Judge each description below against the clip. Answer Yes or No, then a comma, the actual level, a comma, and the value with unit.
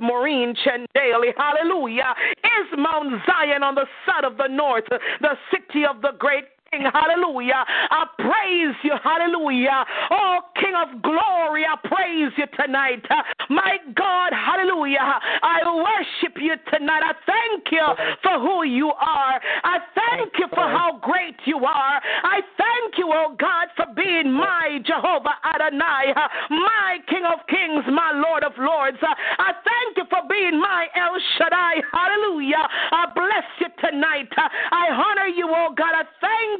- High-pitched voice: Yes, very high, 320 Hz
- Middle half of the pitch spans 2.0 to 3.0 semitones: No, average, 3.9 semitones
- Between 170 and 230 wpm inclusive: No, average, 150 wpm